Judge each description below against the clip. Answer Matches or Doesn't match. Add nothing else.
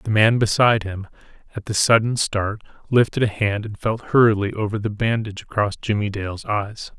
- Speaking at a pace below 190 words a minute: Matches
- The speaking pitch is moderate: Doesn't match